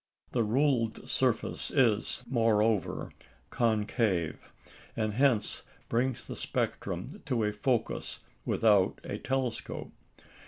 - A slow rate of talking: Yes, slow, 95 wpm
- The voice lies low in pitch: Yes, low, 115 Hz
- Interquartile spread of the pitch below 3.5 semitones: Yes, average, 2.9 semitones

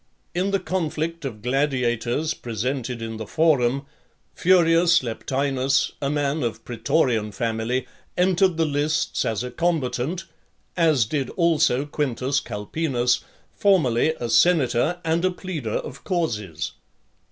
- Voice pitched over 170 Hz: No, medium, 140 Hz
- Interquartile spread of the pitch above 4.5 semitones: Yes, wide, 5.5 semitones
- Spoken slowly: Yes, slow, 120 wpm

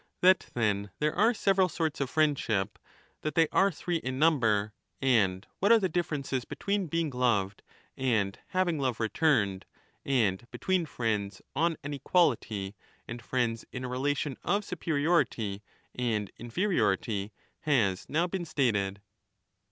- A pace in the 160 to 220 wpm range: No, average, 140 wpm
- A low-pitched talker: Yes, low, 130 Hz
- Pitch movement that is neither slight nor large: No, wide, 7.4 semitones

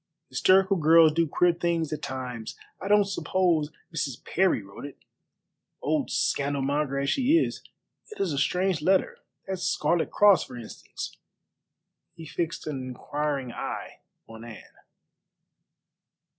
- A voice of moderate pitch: Yes, medium, 155 Hz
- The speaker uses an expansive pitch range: No, average, 4.7 semitones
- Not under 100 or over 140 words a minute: Yes, slow, 135 wpm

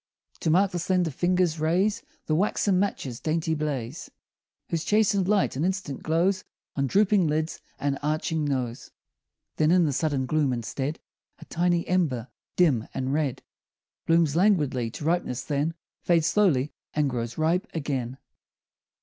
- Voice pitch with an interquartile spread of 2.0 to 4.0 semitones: No, average, 4.5 semitones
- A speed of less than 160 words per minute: Yes, average, 145 wpm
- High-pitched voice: No, medium, 155 Hz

